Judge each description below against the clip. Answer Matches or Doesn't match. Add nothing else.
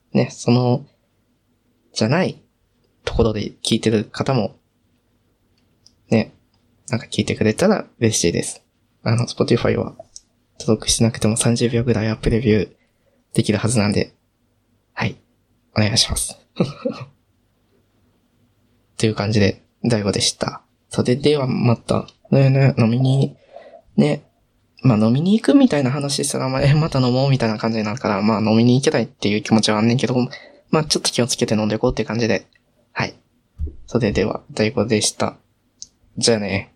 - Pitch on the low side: Matches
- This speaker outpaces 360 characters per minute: Doesn't match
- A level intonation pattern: Matches